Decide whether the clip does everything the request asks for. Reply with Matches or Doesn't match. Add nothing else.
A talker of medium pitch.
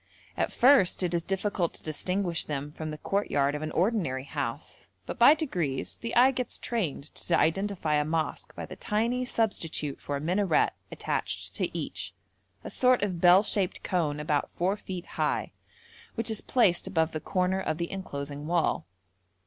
Matches